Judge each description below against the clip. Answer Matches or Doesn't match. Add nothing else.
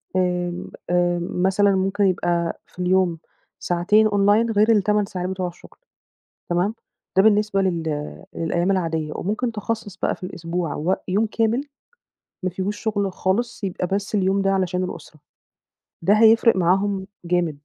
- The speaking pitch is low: Doesn't match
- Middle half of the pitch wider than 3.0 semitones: Doesn't match